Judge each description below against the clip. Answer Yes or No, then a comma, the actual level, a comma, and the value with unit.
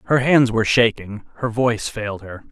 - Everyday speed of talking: Yes, average, 190 wpm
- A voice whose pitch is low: Yes, low, 115 Hz